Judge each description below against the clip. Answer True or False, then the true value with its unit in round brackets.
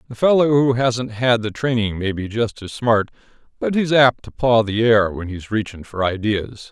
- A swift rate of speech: True (215 wpm)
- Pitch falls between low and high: False (115 Hz)